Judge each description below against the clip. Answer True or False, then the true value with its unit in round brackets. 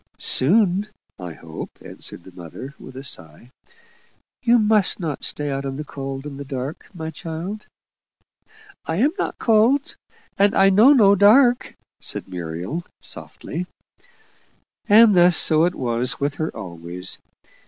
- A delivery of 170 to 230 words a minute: False (145 wpm)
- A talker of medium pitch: True (160 Hz)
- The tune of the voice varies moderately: False (7.9 semitones)